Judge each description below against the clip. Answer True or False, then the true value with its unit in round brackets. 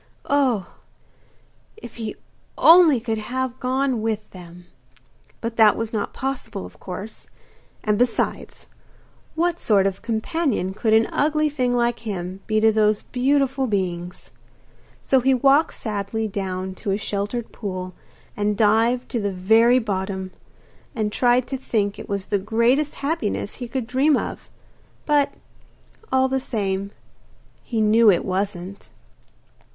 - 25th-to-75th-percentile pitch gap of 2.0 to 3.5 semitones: False (4.3 semitones)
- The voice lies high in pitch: True (220 Hz)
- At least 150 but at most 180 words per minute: False (140 wpm)